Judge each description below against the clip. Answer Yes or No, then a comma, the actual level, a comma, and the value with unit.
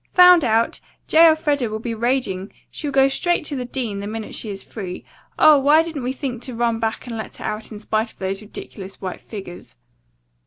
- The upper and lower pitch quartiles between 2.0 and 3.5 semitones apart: No, average, 4.5 semitones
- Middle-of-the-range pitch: No, high, 235 Hz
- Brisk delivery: Yes, fast, 210 wpm